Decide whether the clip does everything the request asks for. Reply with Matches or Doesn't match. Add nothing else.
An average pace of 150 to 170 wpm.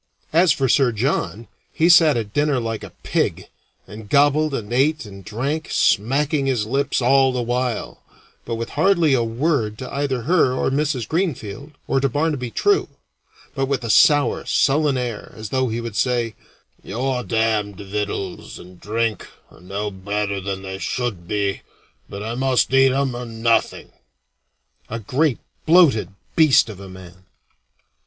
Matches